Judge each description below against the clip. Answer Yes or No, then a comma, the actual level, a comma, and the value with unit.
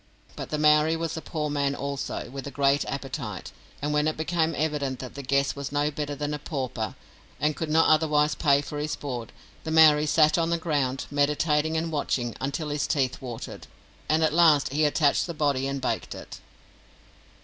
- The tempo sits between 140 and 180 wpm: No, average, 195 wpm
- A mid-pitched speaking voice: Yes, medium, 150 Hz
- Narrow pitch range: Yes, narrow, 2.0 semitones